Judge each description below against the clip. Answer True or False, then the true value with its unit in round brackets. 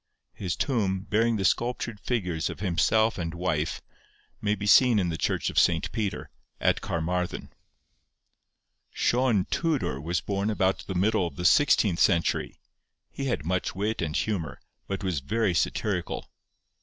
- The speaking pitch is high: False (95 Hz)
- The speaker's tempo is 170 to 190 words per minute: False (150 wpm)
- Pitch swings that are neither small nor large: True (4.2 semitones)